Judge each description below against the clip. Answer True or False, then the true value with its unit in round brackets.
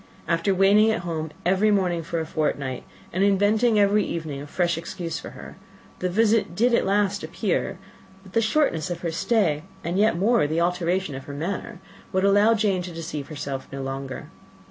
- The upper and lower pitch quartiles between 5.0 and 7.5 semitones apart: False (4.2 semitones)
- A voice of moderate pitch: True (180 Hz)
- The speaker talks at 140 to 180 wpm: False (190 wpm)